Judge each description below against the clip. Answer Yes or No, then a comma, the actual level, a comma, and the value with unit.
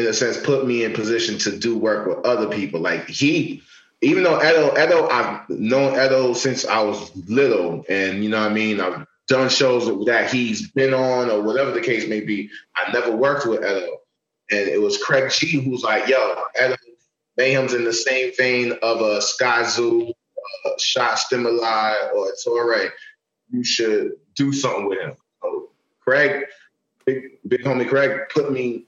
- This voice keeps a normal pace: Yes, average, 185 wpm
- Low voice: Yes, low, 130 Hz